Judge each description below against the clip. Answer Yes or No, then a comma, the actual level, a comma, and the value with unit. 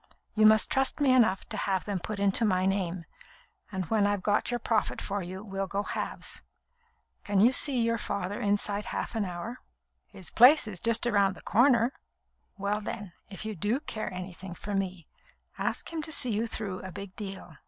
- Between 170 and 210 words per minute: Yes, average, 195 wpm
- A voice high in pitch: Yes, high, 205 Hz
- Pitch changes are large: No, average, 3.0 semitones